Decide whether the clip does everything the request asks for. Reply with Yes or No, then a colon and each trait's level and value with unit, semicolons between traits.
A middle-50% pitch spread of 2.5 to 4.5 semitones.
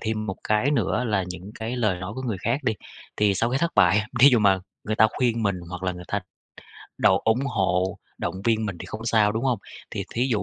Yes: average, 3.4 semitones